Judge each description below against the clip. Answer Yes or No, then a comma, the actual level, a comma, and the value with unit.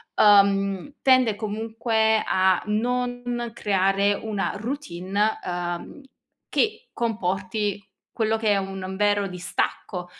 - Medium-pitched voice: No, high, 205 Hz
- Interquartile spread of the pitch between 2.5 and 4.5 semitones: Yes, average, 2.8 semitones